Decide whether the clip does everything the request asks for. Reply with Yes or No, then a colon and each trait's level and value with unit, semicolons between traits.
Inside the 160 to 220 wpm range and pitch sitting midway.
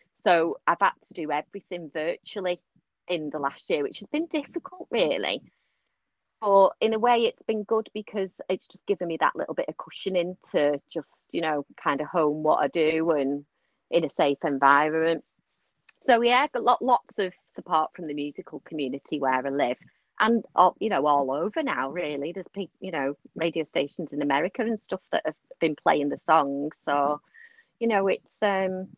Yes: average, 190 wpm; medium, 180 Hz